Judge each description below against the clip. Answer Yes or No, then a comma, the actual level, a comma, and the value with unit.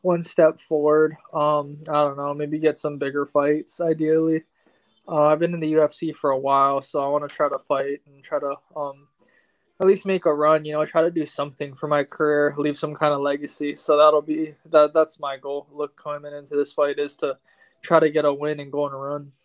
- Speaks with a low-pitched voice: No, medium, 150 Hz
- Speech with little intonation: Yes, narrow, 1.4 semitones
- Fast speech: Yes, fast, 235 wpm